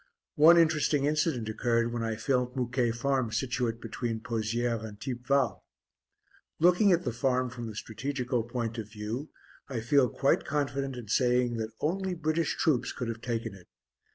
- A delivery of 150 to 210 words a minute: Yes, average, 160 wpm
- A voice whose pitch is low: Yes, low, 125 Hz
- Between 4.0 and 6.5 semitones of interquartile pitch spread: No, average, 3.3 semitones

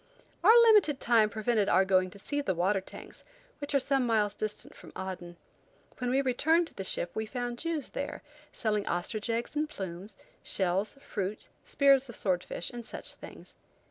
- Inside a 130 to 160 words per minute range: No, average, 180 wpm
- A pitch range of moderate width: No, wide, 6.2 semitones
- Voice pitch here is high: Yes, high, 220 Hz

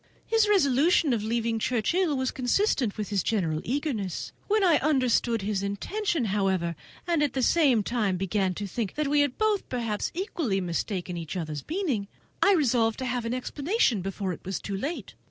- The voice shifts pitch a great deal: Yes, wide, 7.0 semitones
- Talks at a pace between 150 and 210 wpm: Yes, average, 185 wpm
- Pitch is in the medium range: No, high, 235 Hz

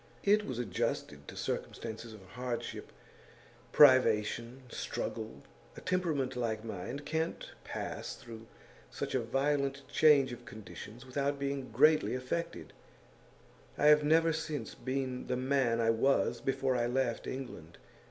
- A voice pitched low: Yes, low, 130 Hz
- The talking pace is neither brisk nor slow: No, slow, 130 wpm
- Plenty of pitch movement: No, average, 3.4 semitones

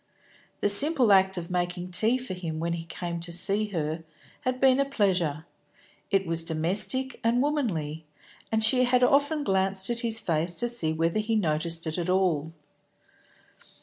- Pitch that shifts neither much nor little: No, wide, 6.0 semitones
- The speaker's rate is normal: Yes, average, 170 wpm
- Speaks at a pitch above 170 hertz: Yes, high, 190 Hz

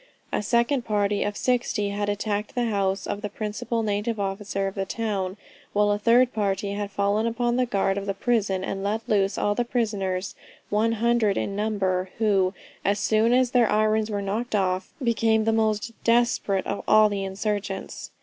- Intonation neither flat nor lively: No, narrow, 2.3 semitones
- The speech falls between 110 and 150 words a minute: No, average, 185 wpm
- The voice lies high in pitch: Yes, high, 210 Hz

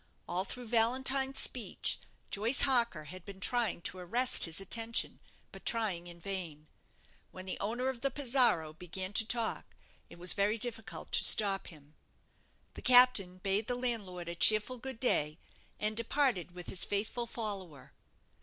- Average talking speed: Yes, average, 155 wpm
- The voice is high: Yes, high, 210 Hz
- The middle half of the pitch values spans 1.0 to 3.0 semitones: No, average, 5.1 semitones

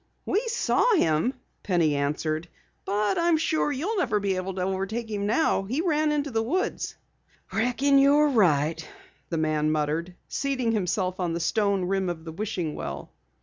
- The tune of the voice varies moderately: No, wide, 8.4 semitones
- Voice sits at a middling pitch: No, high, 200 Hz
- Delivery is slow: No, average, 150 wpm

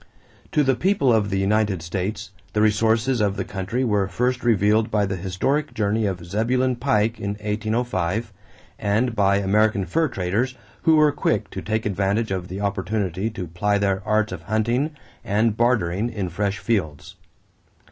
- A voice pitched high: No, low, 105 Hz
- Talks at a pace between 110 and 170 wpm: Yes, average, 165 wpm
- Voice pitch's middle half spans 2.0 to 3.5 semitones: Yes, average, 3.1 semitones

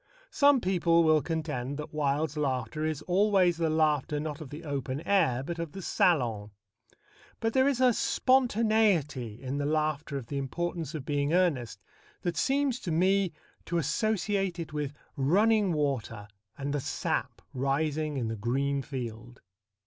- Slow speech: No, average, 155 wpm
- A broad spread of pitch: No, average, 4.6 semitones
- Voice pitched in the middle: Yes, medium, 155 Hz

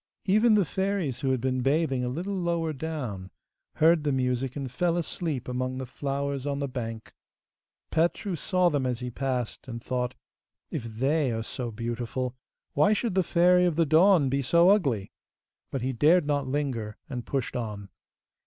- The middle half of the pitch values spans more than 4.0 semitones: Yes, average, 5.0 semitones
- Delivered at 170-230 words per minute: Yes, average, 175 wpm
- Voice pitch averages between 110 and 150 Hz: Yes, low, 135 Hz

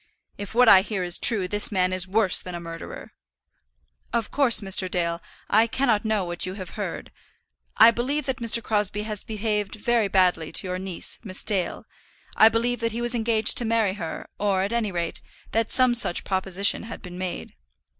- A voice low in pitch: No, high, 205 Hz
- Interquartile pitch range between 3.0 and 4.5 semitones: Yes, average, 3.6 semitones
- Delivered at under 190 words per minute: No, average, 195 wpm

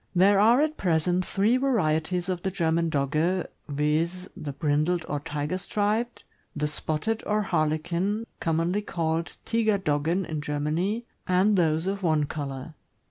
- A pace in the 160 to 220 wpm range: No, average, 140 wpm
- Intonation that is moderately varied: Yes, average, 4.3 semitones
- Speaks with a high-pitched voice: No, medium, 170 Hz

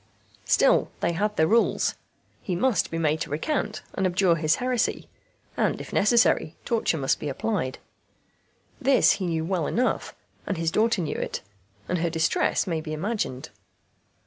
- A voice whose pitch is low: No, medium, 175 Hz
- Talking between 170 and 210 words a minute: No, average, 160 wpm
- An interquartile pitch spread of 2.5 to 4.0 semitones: No, wide, 5.4 semitones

